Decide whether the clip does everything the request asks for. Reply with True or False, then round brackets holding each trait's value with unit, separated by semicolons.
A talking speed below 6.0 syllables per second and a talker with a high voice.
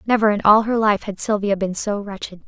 True (5.7 syllables/s; 205 Hz)